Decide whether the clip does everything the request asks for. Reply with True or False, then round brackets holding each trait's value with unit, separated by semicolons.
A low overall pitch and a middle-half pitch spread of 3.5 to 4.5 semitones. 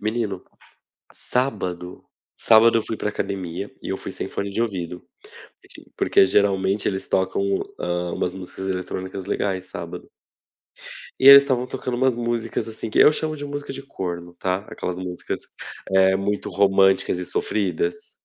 True (100 Hz; 4.1 semitones)